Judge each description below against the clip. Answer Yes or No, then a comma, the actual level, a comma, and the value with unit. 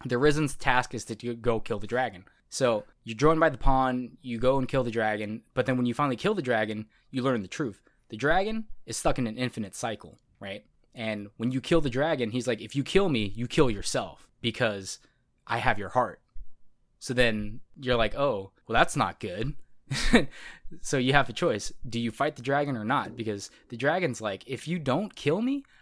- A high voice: No, low, 125 Hz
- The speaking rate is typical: No, fast, 215 wpm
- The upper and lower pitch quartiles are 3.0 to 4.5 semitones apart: Yes, average, 3.7 semitones